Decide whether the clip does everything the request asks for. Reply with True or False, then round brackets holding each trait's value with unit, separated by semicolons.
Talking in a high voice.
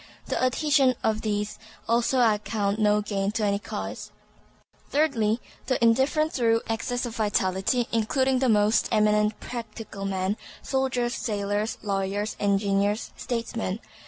True (220 Hz)